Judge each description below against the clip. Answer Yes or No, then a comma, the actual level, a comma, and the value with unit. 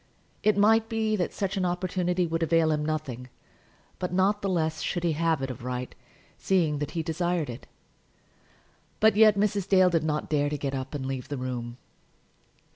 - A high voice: No, medium, 165 Hz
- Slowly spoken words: No, average, 185 wpm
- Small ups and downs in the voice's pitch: No, average, 4.6 semitones